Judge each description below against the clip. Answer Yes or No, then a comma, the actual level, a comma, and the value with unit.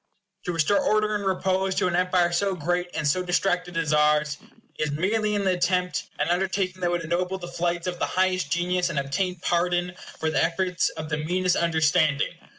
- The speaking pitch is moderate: Yes, medium, 180 Hz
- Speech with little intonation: Yes, narrow, 1.9 semitones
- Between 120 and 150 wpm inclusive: No, average, 195 wpm